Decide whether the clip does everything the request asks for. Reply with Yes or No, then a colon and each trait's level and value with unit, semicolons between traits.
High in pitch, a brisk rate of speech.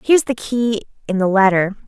No: high, 215 Hz; average, 190 wpm